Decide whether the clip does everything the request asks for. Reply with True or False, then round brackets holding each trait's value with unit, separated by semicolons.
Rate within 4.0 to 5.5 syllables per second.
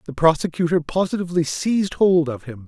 False (5.9 syllables/s)